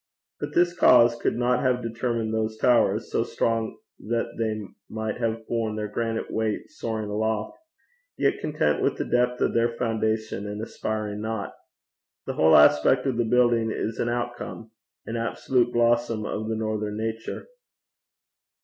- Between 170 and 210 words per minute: No, average, 155 wpm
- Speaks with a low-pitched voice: Yes, low, 115 Hz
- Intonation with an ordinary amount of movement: No, narrow, 1.4 semitones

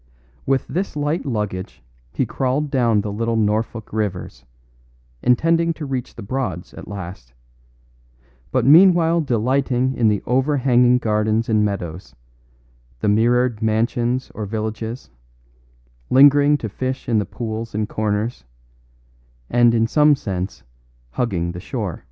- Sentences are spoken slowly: Yes, slow, 130 wpm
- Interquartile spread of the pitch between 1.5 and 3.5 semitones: No, average, 4.0 semitones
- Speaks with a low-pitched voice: Yes, low, 115 Hz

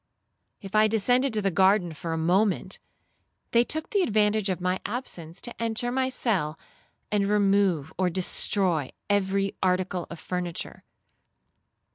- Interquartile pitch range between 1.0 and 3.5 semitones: Yes, average, 3.2 semitones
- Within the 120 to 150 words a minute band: Yes, average, 140 wpm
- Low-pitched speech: No, high, 195 Hz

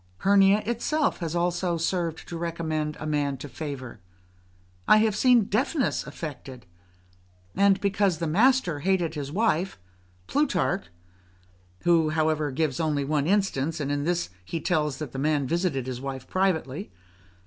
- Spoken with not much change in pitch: No, average, 4.9 semitones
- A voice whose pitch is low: No, medium, 165 Hz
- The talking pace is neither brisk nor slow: Yes, average, 150 wpm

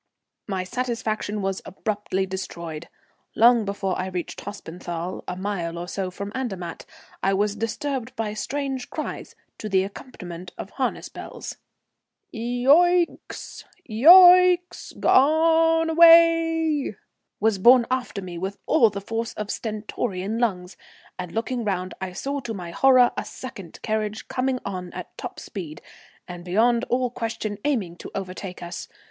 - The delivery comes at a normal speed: Yes, average, 145 wpm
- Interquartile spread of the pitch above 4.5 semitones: Yes, wide, 5.5 semitones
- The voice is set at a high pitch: Yes, high, 215 Hz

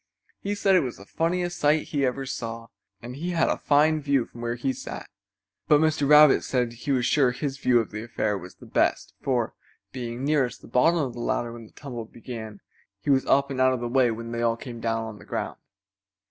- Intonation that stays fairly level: No, average, 3.7 semitones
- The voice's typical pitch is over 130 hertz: No, low, 125 Hz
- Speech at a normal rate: No, fast, 230 wpm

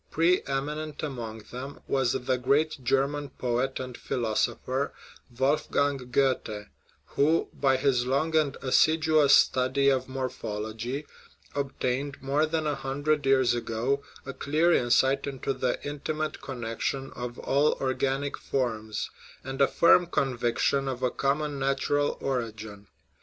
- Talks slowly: Yes, slow, 130 wpm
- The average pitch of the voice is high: No, low, 135 Hz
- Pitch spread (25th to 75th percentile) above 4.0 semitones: No, narrow, 2.4 semitones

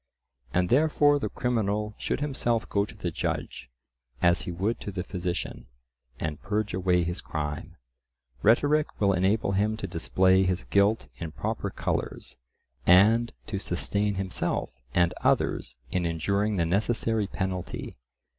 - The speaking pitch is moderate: No, low, 100 Hz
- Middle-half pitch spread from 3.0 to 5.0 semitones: Yes, average, 3.4 semitones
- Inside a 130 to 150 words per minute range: Yes, average, 140 wpm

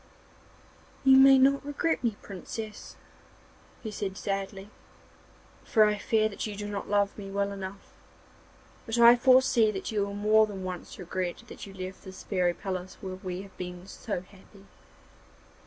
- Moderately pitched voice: No, high, 200 Hz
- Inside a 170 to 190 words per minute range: No, average, 160 wpm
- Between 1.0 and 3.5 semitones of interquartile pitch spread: Yes, narrow, 2.5 semitones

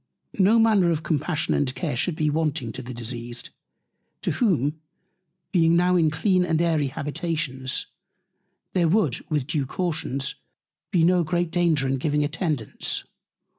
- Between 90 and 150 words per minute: Yes, average, 145 wpm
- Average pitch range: Yes, average, 4.1 semitones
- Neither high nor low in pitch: Yes, medium, 155 Hz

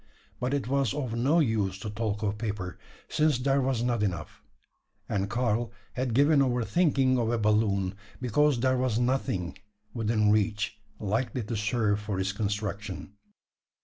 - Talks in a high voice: No, low, 115 Hz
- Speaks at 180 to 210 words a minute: No, average, 155 wpm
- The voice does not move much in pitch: No, average, 3.7 semitones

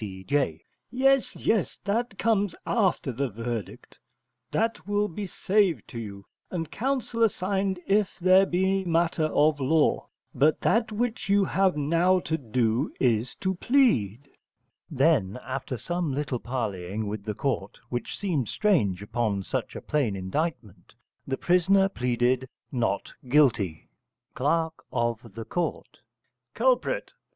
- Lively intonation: Yes, wide, 8.7 semitones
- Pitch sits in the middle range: Yes, medium, 150 Hz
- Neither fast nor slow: No, slow, 125 wpm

